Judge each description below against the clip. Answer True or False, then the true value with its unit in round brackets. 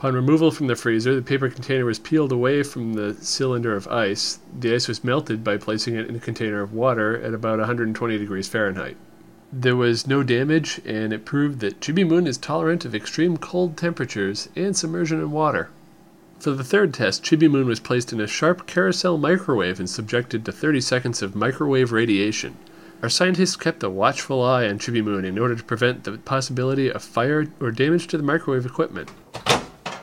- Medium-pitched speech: False (130 Hz)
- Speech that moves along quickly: False (195 wpm)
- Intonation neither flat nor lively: False (5.7 semitones)